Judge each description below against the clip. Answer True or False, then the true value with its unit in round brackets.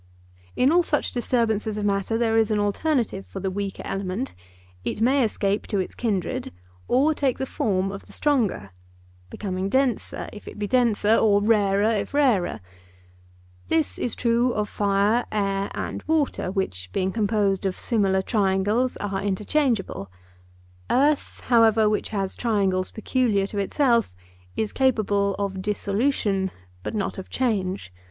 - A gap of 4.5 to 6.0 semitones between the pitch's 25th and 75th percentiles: False (3.4 semitones)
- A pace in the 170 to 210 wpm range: False (145 wpm)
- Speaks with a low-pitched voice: False (205 Hz)